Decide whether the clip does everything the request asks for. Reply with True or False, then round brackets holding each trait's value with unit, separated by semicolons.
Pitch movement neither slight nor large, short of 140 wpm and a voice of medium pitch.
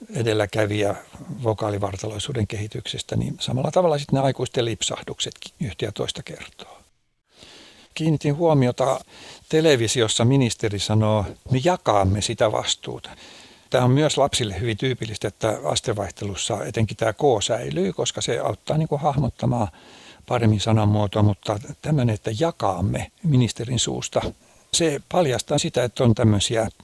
False (5.0 semitones; 125 wpm; 120 Hz)